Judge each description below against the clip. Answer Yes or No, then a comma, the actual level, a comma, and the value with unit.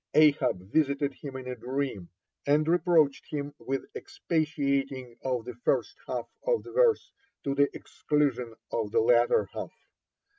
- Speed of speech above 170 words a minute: No, average, 145 wpm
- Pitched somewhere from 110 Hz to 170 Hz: Yes, medium, 140 Hz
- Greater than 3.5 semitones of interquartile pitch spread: No, average, 3.2 semitones